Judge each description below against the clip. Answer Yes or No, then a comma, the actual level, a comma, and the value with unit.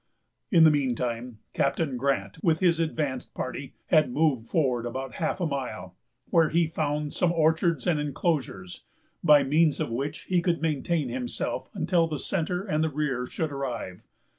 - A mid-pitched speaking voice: Yes, medium, 150 Hz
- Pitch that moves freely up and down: No, average, 4.2 semitones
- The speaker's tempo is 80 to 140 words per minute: No, average, 165 wpm